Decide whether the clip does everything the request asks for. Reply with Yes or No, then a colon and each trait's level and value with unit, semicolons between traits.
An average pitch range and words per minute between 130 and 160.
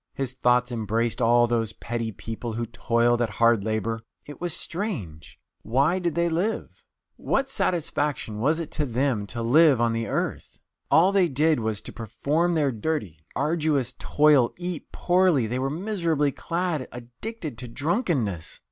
No: wide, 6.2 semitones; average, 155 wpm